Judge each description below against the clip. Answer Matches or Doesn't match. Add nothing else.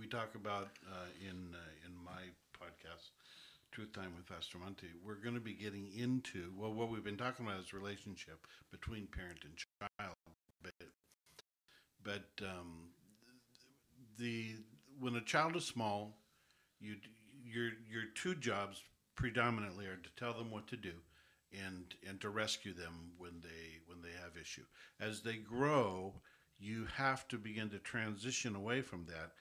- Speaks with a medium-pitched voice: Doesn't match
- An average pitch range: Matches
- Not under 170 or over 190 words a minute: Doesn't match